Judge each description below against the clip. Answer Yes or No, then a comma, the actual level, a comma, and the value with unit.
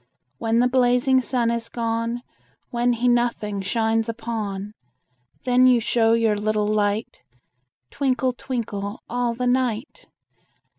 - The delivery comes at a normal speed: No, slow, 120 wpm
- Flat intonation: Yes, narrow, 2.0 semitones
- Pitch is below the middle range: No, high, 235 Hz